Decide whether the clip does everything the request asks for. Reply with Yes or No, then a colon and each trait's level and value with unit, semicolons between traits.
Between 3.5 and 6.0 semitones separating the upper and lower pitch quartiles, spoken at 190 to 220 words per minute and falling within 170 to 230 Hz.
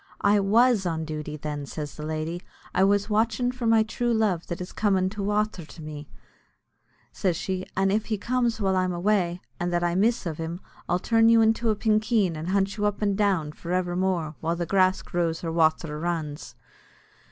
Yes: average, 4.2 semitones; average, 200 wpm; medium, 185 Hz